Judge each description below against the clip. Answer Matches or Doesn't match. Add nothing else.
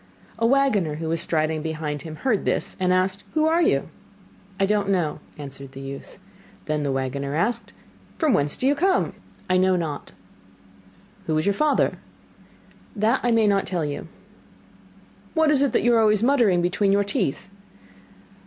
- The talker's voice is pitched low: Doesn't match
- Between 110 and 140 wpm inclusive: Doesn't match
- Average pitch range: Doesn't match